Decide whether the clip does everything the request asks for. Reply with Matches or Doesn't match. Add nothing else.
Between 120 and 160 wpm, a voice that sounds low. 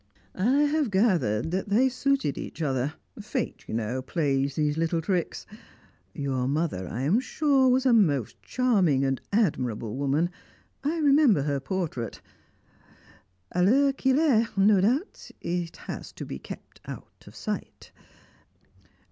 Doesn't match